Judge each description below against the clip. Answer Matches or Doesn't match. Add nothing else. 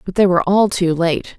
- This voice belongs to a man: Doesn't match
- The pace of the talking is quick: Matches